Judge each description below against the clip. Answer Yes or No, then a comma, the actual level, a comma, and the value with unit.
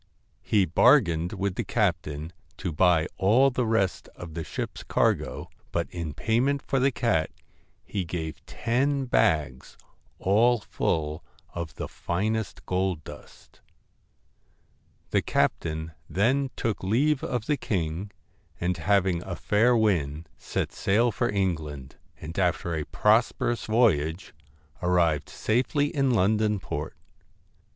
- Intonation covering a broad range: Yes, wide, 6.0 semitones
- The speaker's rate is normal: No, slow, 125 wpm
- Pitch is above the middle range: No, very low, 95 Hz